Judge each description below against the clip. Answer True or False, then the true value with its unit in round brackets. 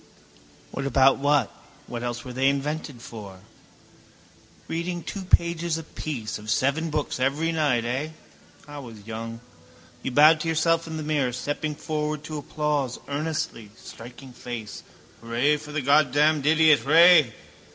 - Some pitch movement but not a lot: True (4.0 semitones)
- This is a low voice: False (145 Hz)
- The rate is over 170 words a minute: False (140 wpm)